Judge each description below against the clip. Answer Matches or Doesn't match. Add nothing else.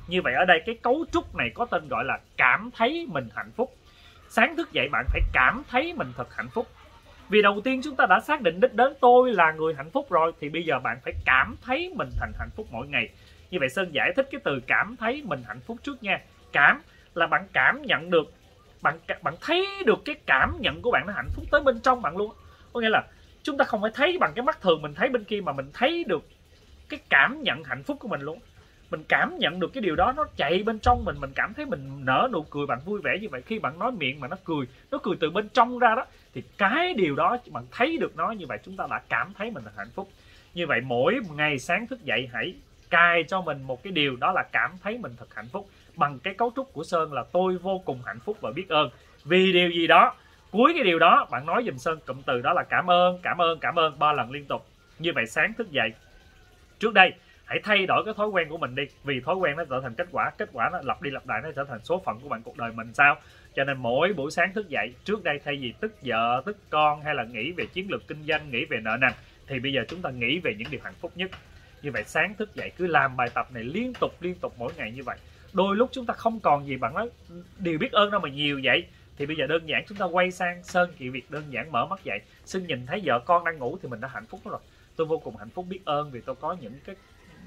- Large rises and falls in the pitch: Matches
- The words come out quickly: Matches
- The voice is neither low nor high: Matches